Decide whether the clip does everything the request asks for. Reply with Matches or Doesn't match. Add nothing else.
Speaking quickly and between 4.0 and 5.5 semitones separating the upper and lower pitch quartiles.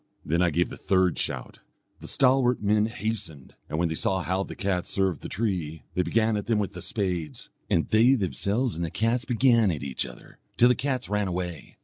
Matches